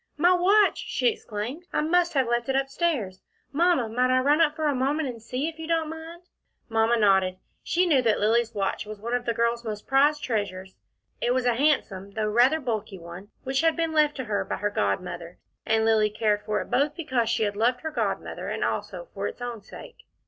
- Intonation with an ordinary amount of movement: No, wide, 6.1 semitones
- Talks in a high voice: Yes, high, 245 Hz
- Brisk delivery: Yes, fast, 220 wpm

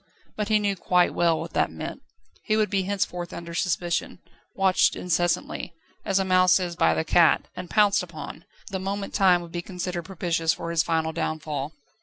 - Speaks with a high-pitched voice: No, medium, 180 Hz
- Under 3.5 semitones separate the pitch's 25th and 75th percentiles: Yes, narrow, 2.5 semitones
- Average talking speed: Yes, average, 185 wpm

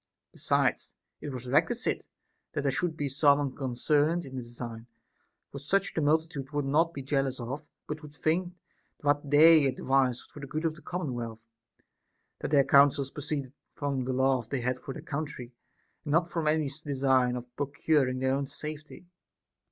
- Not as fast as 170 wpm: No, average, 175 wpm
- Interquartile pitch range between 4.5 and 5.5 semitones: No, average, 2.8 semitones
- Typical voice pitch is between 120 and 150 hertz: Yes, medium, 140 Hz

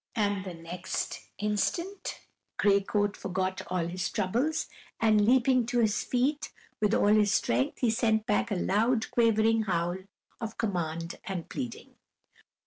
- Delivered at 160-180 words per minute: No, average, 140 wpm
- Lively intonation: No, average, 3.8 semitones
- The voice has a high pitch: Yes, high, 210 Hz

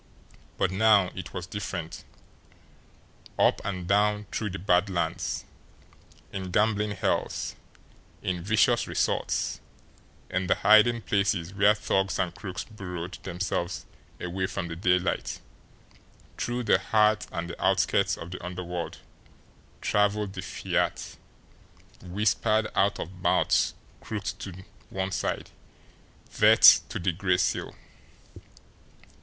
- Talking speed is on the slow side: Yes, slow, 115 wpm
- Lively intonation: No, narrow, 2.6 semitones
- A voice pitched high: No, very low, 95 Hz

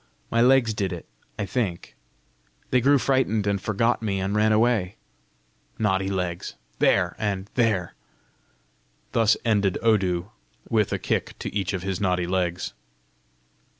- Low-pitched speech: Yes, low, 100 Hz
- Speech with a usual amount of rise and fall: Yes, average, 3.2 semitones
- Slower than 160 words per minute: Yes, average, 140 wpm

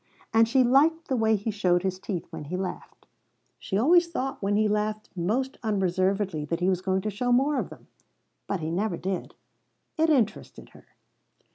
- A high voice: Yes, high, 210 Hz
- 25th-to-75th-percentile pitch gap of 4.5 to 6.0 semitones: Yes, average, 4.9 semitones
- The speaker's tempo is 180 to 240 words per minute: Yes, average, 185 wpm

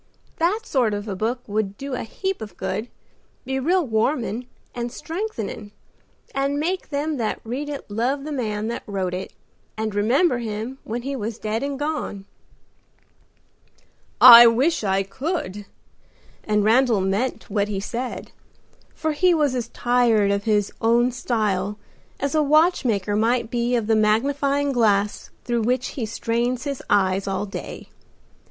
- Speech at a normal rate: Yes, average, 155 wpm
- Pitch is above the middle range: Yes, high, 235 Hz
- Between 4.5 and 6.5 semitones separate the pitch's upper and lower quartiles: Yes, average, 4.8 semitones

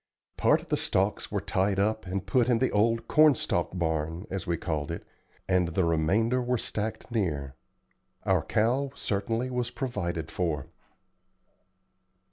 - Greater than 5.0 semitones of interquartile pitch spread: Yes, wide, 5.6 semitones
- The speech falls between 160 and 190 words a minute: No, average, 150 wpm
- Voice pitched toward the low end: Yes, low, 100 Hz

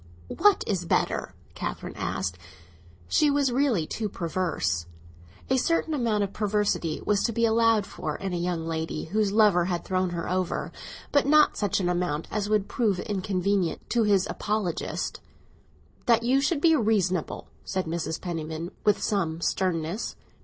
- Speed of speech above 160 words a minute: No, average, 155 wpm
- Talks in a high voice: Yes, high, 195 Hz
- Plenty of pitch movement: No, average, 4.5 semitones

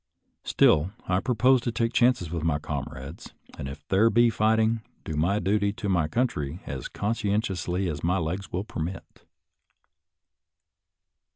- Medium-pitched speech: No, very low, 95 Hz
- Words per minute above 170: No, average, 155 wpm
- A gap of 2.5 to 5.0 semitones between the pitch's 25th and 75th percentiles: No, wide, 5.6 semitones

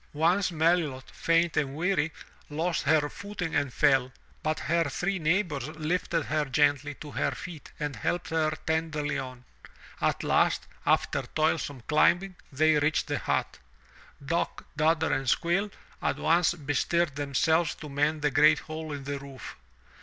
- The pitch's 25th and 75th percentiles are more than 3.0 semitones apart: No, narrow, 2.5 semitones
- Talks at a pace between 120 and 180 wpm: Yes, average, 150 wpm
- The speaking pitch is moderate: Yes, medium, 155 Hz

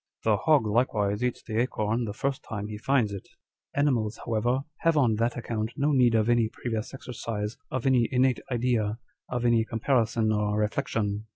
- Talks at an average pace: Yes, average, 175 wpm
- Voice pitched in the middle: No, low, 115 Hz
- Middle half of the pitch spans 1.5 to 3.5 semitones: Yes, narrow, 2.6 semitones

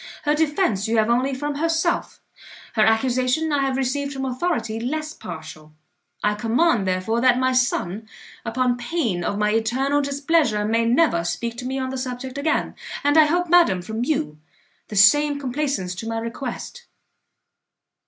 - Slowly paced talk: No, average, 165 wpm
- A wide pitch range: No, average, 4.7 semitones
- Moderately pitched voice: No, very high, 255 Hz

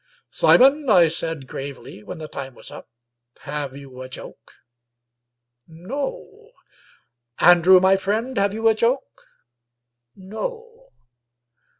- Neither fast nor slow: No, slow, 115 wpm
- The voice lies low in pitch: No, high, 190 Hz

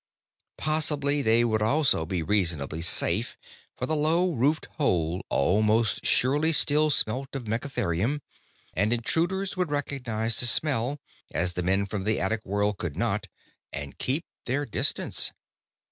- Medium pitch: No, low, 115 Hz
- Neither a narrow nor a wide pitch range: No, wide, 6.6 semitones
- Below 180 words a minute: Yes, average, 140 wpm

